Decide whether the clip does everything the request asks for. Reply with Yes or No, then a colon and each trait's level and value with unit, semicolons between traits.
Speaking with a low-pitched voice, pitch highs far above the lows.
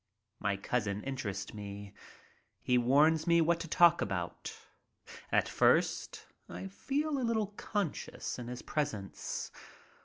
Yes: low, 125 Hz; wide, 9.0 semitones